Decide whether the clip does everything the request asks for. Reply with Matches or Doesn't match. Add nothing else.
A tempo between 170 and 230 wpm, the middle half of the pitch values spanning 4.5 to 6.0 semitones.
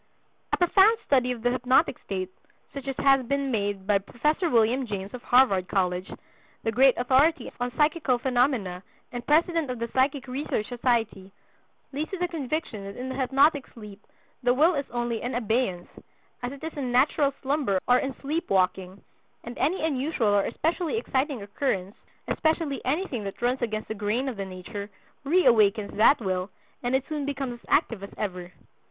Matches